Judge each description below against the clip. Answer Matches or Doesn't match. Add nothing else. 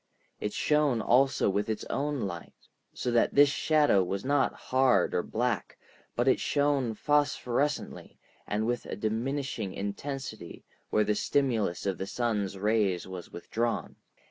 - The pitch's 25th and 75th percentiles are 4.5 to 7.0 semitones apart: Matches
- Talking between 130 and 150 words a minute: Matches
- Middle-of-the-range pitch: Doesn't match